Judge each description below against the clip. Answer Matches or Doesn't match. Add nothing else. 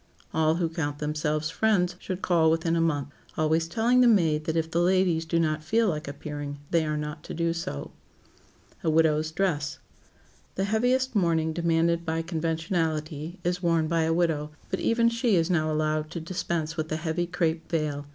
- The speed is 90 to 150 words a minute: Doesn't match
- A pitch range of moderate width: Doesn't match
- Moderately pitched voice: Matches